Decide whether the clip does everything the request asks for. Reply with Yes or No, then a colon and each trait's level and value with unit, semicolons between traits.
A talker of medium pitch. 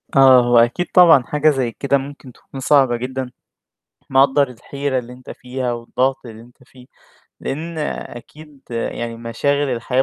No: low, 130 Hz